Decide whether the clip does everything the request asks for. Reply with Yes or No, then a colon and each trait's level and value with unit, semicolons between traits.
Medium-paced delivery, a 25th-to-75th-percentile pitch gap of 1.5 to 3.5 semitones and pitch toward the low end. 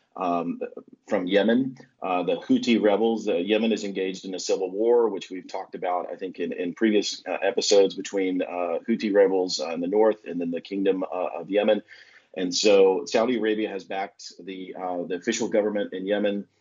Yes: average, 195 wpm; average, 2.9 semitones; low, 100 Hz